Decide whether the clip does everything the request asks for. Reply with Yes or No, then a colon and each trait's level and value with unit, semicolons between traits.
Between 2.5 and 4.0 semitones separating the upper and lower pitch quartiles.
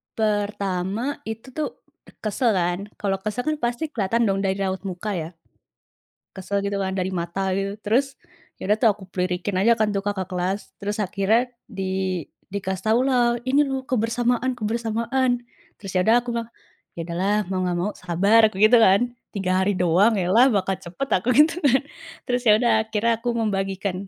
Yes: average, 3.6 semitones